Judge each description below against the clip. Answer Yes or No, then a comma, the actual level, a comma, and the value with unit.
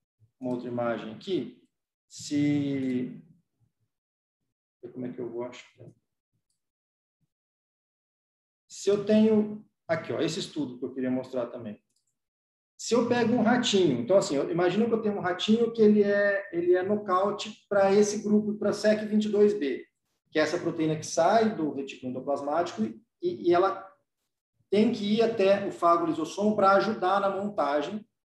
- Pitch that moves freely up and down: Yes, wide, 8.4 semitones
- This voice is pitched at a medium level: Yes, medium, 180 Hz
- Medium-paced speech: Yes, average, 155 wpm